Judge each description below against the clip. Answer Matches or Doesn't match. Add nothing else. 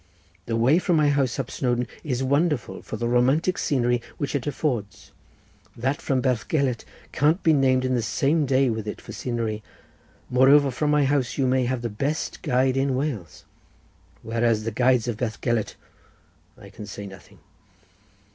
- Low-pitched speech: Matches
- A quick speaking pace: Doesn't match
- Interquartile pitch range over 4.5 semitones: Doesn't match